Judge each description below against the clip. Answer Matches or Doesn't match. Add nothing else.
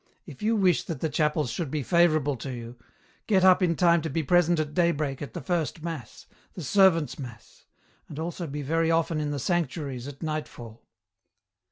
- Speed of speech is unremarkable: Matches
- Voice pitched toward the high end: Doesn't match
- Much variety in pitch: Doesn't match